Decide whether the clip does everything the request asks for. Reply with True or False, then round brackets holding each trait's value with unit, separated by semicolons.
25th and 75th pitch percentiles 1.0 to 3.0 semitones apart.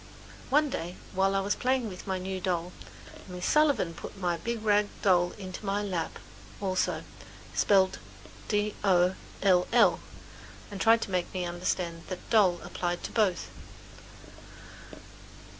True (2.6 semitones)